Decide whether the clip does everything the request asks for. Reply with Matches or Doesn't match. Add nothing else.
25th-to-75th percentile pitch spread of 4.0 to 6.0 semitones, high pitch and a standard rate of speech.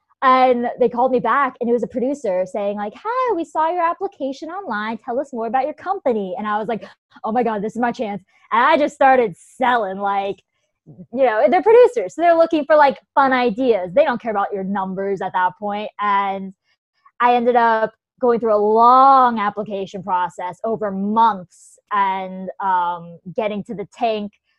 Matches